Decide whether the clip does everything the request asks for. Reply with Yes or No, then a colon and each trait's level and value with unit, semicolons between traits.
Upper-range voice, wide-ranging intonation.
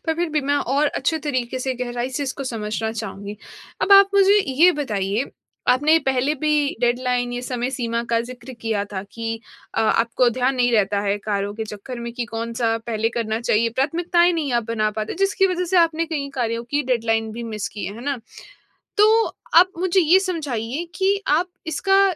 Yes: very high, 250 Hz; wide, 5.7 semitones